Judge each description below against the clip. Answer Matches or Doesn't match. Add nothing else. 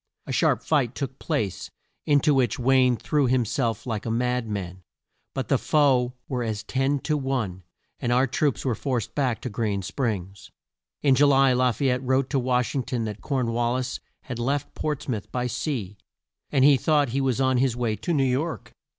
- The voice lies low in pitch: Matches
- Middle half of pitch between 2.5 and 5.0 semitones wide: Matches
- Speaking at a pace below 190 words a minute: Doesn't match